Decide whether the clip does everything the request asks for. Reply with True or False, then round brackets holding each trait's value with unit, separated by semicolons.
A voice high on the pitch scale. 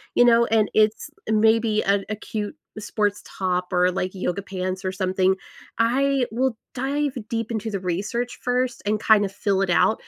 True (215 Hz)